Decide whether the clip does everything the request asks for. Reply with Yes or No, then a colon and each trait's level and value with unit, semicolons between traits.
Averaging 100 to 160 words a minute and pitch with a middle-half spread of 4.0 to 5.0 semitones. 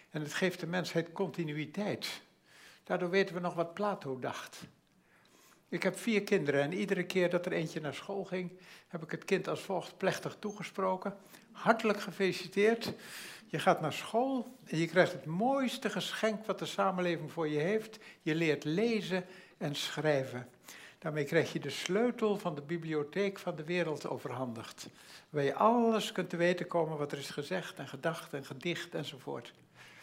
No: average, 170 wpm; average, 4.3 semitones